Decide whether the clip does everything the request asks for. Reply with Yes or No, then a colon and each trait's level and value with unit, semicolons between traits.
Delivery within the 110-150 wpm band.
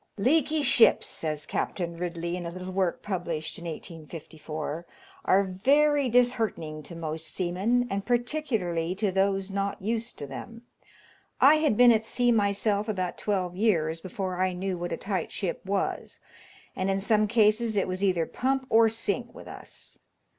No: average, 160 wpm